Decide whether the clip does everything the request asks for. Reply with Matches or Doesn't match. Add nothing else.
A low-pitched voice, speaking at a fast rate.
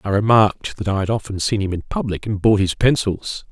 Matches